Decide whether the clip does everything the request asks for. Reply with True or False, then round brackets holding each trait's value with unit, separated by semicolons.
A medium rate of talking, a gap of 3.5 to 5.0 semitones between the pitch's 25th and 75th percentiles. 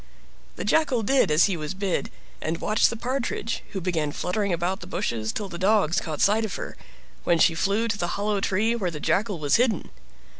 False (210 wpm; 4.4 semitones)